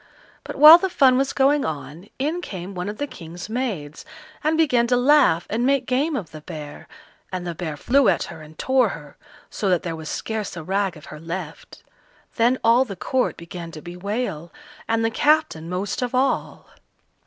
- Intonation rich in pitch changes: Yes, wide, 7.6 semitones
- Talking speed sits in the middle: Yes, average, 195 wpm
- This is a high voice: Yes, high, 205 Hz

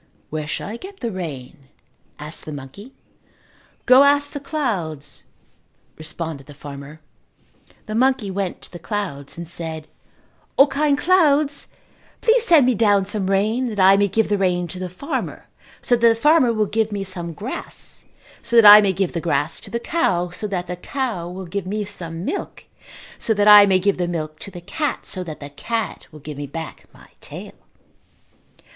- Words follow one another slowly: No, average, 190 wpm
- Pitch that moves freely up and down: Yes, wide, 5.8 semitones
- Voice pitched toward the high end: Yes, high, 195 Hz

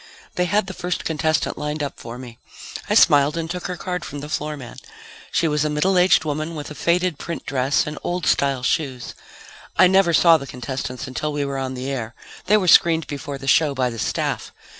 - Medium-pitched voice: Yes, medium, 150 Hz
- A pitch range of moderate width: Yes, average, 3.9 semitones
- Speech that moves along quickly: Yes, fast, 220 wpm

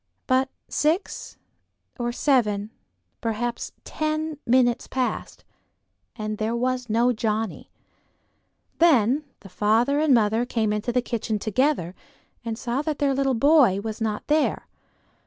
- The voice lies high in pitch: Yes, high, 240 Hz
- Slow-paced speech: Yes, slow, 125 wpm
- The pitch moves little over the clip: No, average, 4.0 semitones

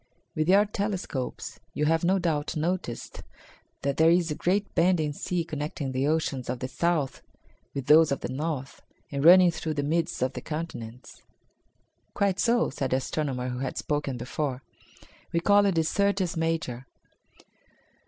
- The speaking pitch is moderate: Yes, medium, 155 Hz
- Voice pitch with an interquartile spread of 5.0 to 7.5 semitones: No, average, 4.3 semitones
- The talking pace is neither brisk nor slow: Yes, average, 165 wpm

